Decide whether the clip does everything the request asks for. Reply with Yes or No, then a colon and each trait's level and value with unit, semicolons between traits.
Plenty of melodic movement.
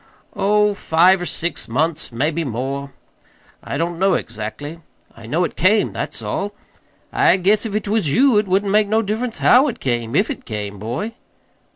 Yes: wide, 7.2 semitones